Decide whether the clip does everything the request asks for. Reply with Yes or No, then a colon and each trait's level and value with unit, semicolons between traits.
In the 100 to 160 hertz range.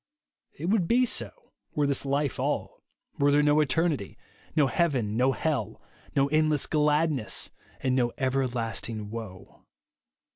Yes: medium, 140 Hz